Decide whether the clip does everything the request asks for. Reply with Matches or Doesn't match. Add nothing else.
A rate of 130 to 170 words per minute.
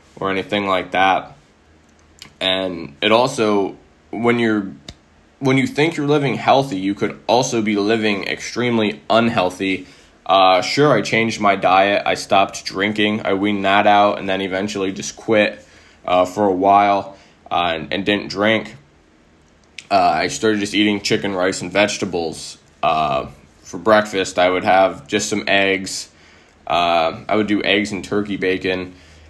Matches